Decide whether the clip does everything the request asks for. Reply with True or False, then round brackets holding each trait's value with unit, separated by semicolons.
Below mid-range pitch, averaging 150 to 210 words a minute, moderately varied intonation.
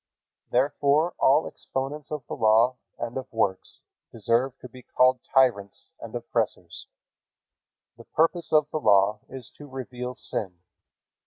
False (130 Hz; 135 wpm; 3.6 semitones)